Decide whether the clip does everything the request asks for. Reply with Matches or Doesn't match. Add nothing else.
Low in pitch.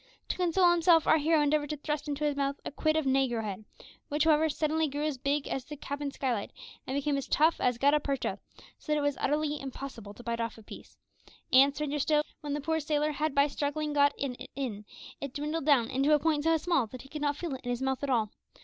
Doesn't match